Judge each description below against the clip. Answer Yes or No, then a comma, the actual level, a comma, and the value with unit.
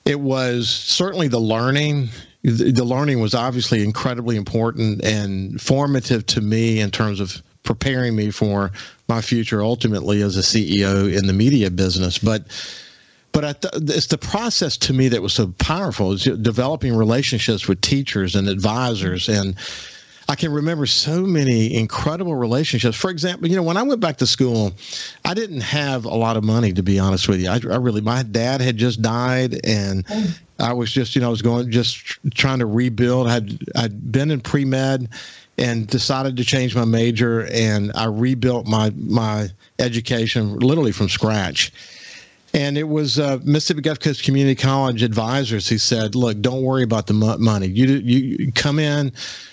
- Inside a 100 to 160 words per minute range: No, average, 175 wpm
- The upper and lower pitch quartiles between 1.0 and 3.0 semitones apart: No, average, 3.8 semitones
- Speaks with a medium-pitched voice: No, low, 120 Hz